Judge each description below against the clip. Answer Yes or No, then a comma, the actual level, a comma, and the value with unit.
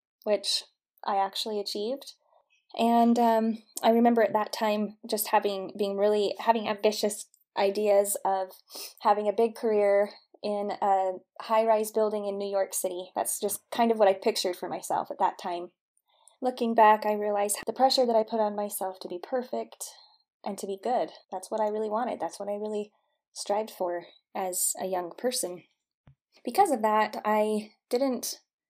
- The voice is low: No, high, 210 Hz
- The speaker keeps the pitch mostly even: Yes, narrow, 2.2 semitones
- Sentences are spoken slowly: No, average, 170 wpm